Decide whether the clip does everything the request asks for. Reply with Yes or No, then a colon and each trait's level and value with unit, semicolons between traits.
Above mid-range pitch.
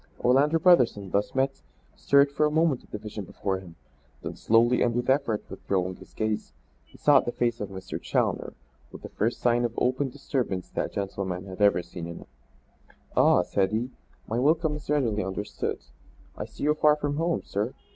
No: low, 120 Hz